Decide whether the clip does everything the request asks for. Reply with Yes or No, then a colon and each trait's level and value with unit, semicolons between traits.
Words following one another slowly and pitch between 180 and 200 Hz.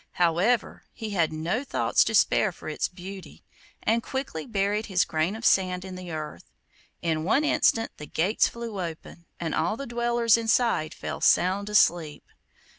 No: average, 165 wpm; high, 190 Hz